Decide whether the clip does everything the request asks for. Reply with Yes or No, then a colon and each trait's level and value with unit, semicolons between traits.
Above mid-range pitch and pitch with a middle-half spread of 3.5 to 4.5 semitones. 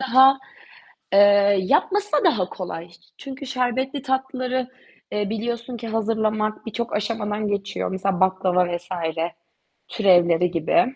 No: high, 215 Hz; average, 5.0 semitones